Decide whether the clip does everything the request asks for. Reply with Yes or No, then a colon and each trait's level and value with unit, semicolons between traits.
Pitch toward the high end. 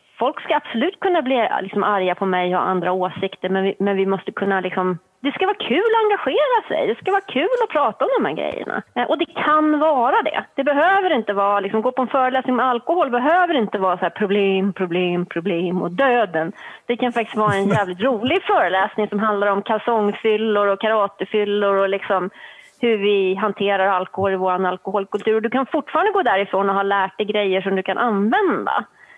Yes: high, 210 Hz